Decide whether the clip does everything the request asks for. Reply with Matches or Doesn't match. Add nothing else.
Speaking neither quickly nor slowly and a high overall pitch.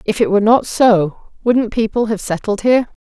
Matches